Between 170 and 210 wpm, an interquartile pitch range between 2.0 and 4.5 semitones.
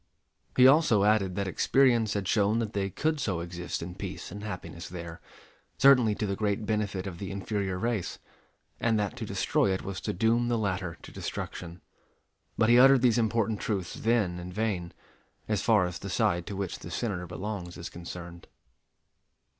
Yes: average, 180 wpm; average, 3.8 semitones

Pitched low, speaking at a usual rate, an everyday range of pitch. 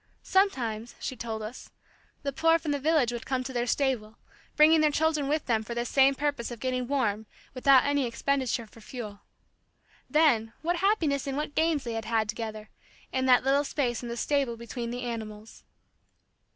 No: very high, 255 Hz; average, 180 wpm; average, 3.7 semitones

